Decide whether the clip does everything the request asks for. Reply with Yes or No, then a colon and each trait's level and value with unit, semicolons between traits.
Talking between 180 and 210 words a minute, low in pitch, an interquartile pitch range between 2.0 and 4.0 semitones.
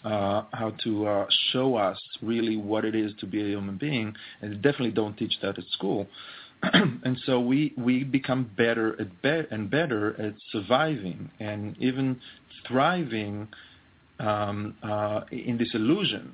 No: average, 160 wpm; low, 110 Hz; average, 3.3 semitones